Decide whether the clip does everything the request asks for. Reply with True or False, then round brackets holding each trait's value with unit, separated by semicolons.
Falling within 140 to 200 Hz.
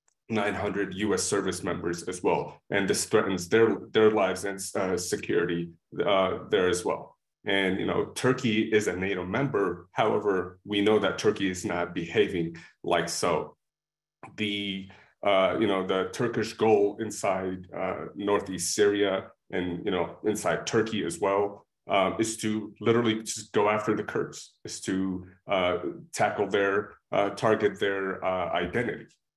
False (100 Hz)